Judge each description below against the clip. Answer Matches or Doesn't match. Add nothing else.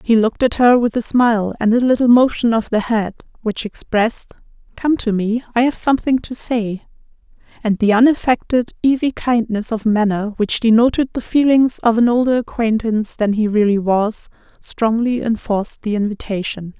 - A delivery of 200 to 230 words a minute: Doesn't match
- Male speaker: Doesn't match